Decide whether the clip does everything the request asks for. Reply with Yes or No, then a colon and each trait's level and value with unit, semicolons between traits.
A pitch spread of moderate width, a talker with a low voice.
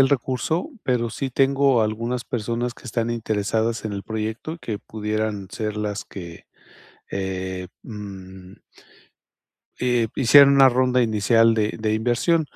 Yes: average, 3.1 semitones; low, 115 Hz